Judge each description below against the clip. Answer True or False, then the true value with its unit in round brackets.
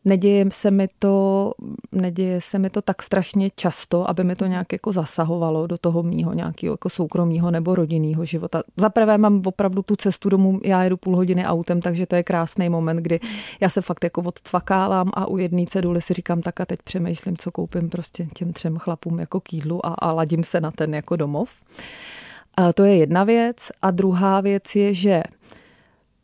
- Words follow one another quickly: True (190 wpm)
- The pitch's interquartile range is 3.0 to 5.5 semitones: False (2.5 semitones)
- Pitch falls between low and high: True (180 Hz)